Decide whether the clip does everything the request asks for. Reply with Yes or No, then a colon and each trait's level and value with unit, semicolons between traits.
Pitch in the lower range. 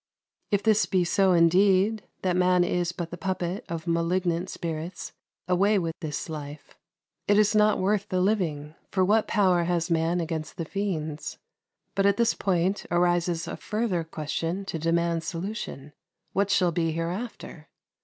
No: medium, 175 Hz